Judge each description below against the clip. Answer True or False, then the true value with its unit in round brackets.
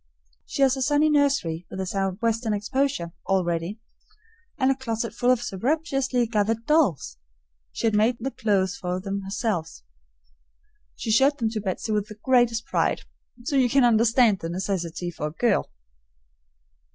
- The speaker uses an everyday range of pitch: True (5.0 semitones)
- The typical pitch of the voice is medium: False (225 Hz)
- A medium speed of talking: True (160 wpm)